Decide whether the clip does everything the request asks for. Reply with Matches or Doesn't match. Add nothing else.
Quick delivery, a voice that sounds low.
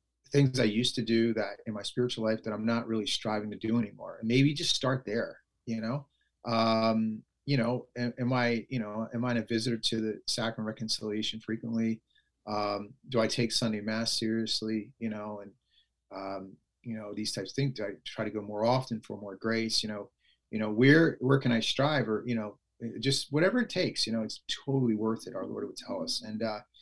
Matches